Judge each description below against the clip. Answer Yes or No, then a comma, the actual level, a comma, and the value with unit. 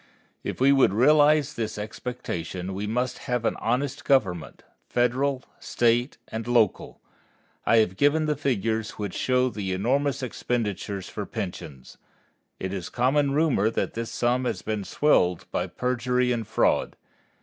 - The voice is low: Yes, low, 120 Hz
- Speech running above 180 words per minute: No, average, 145 wpm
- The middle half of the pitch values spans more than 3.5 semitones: Yes, average, 4.2 semitones